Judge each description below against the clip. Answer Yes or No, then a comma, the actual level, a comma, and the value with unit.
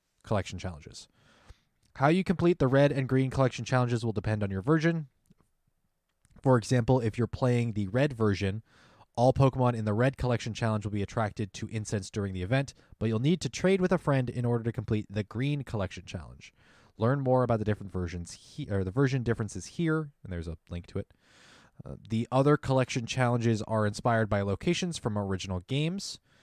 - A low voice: Yes, low, 115 Hz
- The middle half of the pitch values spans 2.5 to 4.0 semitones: No, average, 4.4 semitones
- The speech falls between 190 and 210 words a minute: Yes, average, 195 wpm